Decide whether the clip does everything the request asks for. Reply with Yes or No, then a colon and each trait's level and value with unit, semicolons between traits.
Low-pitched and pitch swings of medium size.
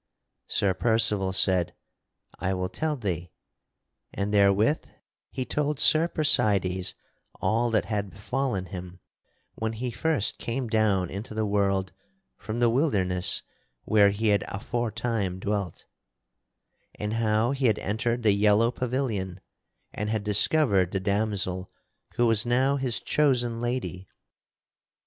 Yes: low, 105 Hz; average, 3.6 semitones